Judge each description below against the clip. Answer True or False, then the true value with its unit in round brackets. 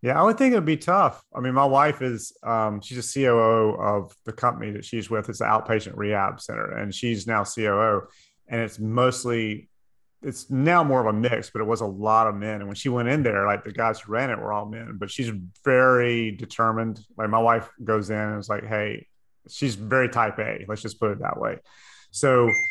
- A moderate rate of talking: False (230 wpm)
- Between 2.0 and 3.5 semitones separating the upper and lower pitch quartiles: True (3.1 semitones)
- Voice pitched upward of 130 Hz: False (115 Hz)